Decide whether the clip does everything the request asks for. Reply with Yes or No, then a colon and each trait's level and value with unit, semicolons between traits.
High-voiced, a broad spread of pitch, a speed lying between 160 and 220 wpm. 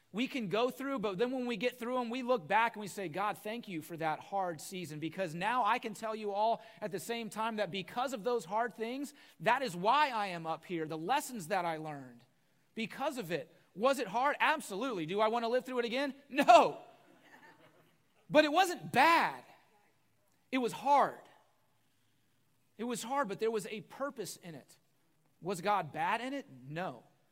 Yes: high, 220 Hz; wide, 6.5 semitones; average, 200 wpm